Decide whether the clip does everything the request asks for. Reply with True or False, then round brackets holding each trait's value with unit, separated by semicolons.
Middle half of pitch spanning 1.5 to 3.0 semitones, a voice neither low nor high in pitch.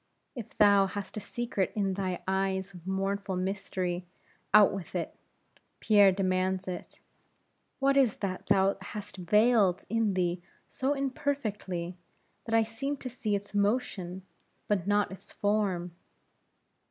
False (2.5 semitones; 200 Hz)